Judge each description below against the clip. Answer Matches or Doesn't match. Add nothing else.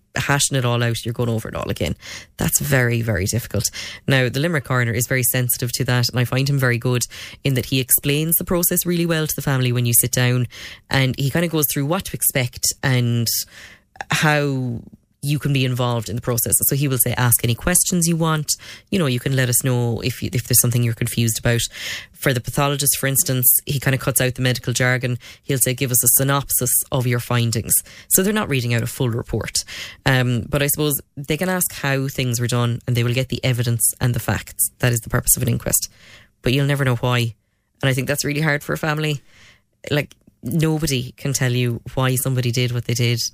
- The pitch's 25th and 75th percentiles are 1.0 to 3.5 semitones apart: Matches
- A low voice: Matches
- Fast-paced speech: Matches